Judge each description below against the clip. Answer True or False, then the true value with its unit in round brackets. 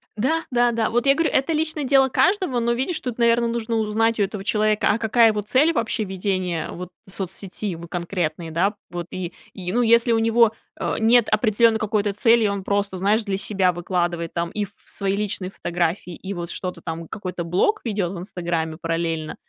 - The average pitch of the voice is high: True (205 Hz)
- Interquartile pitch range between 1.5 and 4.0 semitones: False (4.4 semitones)